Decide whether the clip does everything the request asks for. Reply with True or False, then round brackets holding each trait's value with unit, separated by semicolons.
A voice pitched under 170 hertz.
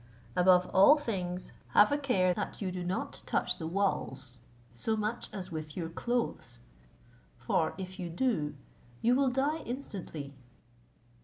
False (185 Hz)